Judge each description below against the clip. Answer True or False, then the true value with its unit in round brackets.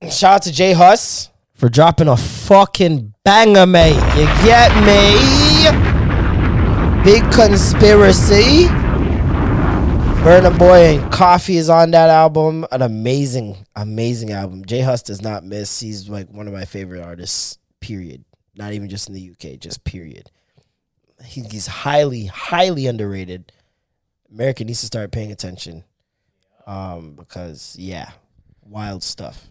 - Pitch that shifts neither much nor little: False (8.1 semitones)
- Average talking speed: False (130 wpm)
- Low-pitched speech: True (110 Hz)